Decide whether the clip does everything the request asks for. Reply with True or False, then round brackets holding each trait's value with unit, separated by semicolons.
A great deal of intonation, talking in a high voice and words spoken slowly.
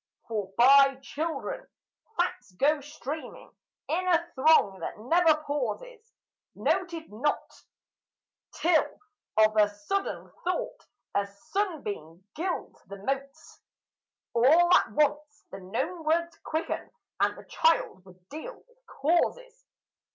True (7.7 semitones; 300 Hz; 115 wpm)